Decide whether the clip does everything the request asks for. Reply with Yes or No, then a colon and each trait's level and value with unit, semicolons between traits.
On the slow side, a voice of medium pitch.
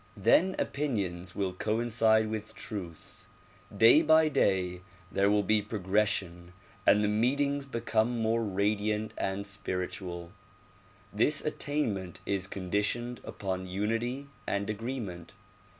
No: slow, 110 wpm; low, 105 Hz